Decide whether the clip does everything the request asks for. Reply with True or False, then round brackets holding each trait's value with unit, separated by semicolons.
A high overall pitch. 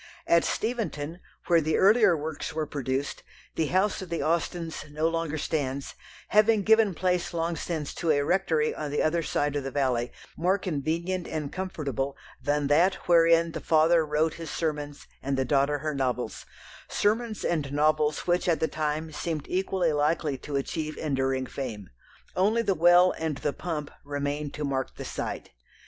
False (155 Hz)